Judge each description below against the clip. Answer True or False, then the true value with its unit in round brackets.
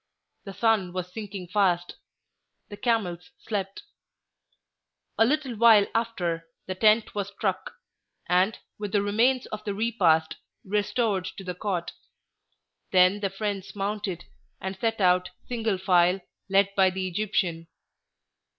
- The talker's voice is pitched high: True (195 Hz)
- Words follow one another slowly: True (130 wpm)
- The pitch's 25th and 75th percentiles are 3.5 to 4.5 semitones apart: False (2.8 semitones)